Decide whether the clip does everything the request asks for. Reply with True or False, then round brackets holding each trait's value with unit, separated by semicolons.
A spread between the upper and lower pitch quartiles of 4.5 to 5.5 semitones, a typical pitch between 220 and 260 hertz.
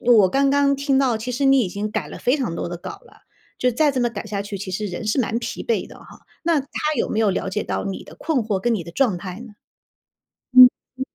True (5.1 semitones; 230 Hz)